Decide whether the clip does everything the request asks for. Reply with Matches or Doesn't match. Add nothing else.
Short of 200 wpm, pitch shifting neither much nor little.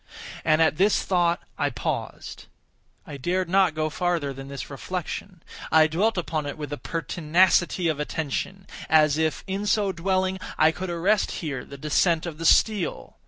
Matches